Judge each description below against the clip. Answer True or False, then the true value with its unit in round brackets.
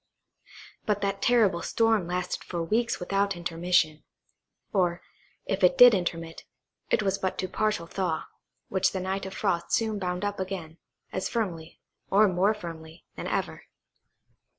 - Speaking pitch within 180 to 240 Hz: True (190 Hz)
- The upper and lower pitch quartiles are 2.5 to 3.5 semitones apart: True (2.9 semitones)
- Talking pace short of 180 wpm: True (150 wpm)